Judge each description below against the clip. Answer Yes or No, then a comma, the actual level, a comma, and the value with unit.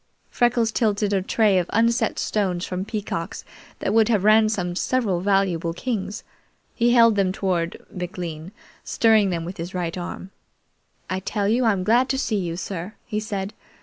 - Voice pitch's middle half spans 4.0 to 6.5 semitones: No, average, 3.5 semitones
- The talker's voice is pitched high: Yes, high, 200 Hz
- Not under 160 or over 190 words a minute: Yes, average, 165 wpm